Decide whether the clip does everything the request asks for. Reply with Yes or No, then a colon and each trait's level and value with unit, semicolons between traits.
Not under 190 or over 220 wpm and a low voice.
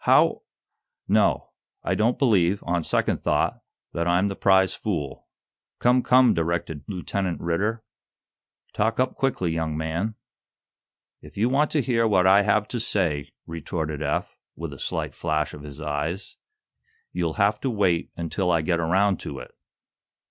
No: average, 155 wpm; very low, 90 Hz